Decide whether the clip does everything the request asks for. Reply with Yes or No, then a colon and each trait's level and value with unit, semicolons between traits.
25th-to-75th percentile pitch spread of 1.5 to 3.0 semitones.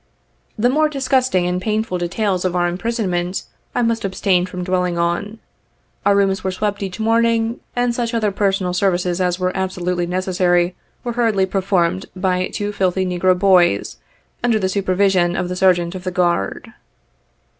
Yes: average, 2.7 semitones